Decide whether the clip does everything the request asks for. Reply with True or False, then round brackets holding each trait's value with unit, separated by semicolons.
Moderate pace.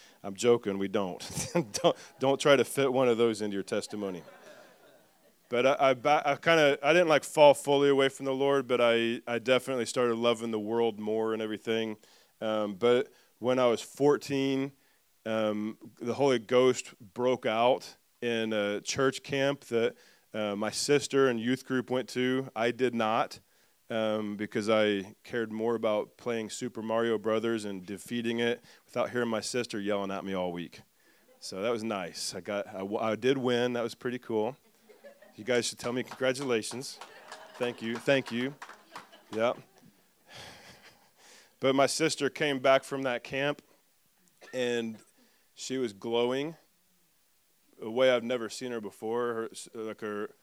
True (165 wpm)